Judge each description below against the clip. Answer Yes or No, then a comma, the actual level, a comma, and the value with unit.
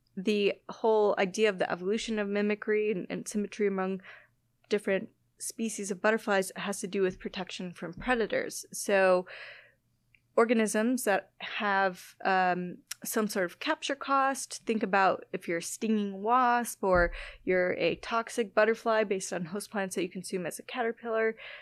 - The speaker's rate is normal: Yes, average, 155 wpm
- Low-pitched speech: No, high, 210 Hz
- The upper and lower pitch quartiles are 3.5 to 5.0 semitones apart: No, average, 3.1 semitones